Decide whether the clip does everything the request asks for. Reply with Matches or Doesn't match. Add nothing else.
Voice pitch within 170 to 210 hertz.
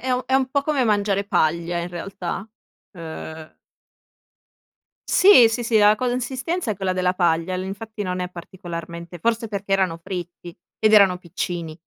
Matches